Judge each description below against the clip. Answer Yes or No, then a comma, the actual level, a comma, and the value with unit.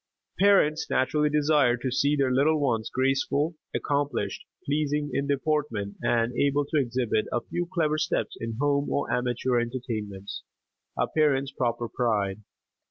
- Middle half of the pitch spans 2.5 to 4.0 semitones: Yes, average, 3.7 semitones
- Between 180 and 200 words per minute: No, average, 140 wpm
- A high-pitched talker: No, low, 135 Hz